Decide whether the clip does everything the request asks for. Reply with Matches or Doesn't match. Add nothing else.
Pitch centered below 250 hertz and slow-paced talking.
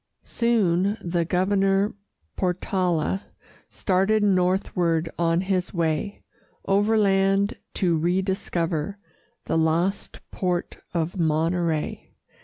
Matches